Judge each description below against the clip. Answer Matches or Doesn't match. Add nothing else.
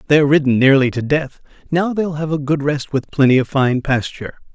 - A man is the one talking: Matches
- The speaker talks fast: Matches